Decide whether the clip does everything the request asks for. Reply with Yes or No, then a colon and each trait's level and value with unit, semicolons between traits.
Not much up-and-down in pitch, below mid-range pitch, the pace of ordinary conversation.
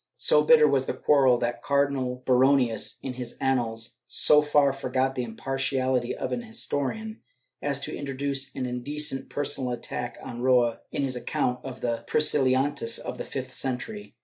Yes: narrow, 2.3 semitones; low, 130 Hz; average, 165 wpm